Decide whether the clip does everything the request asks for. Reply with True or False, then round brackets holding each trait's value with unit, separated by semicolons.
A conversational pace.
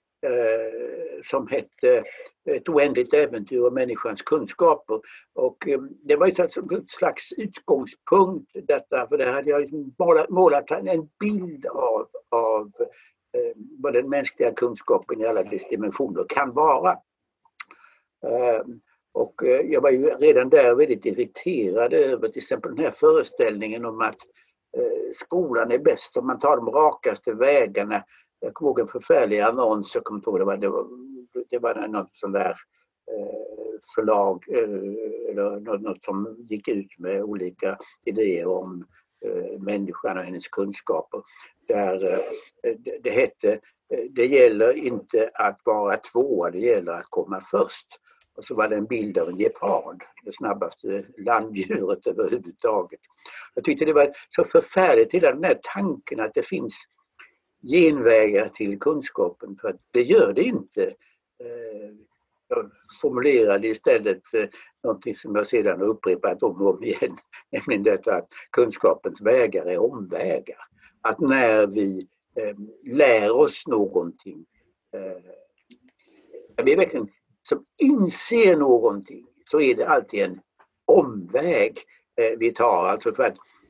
True (135 wpm)